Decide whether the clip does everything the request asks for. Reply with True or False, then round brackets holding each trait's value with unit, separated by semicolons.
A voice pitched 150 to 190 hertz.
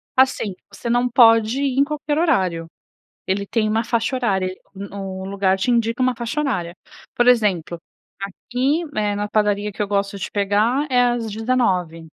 False (215 Hz)